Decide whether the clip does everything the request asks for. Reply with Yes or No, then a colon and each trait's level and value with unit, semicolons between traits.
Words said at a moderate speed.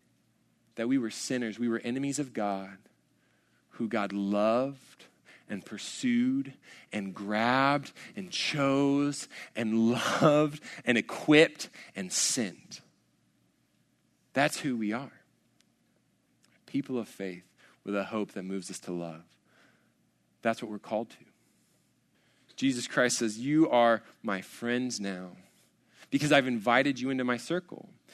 No: slow, 125 wpm